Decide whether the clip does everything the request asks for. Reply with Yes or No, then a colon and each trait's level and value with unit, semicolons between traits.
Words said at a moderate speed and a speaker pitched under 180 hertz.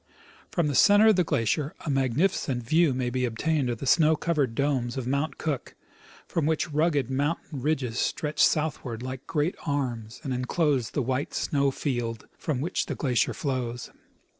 Yes: average, 170 wpm; medium, 140 Hz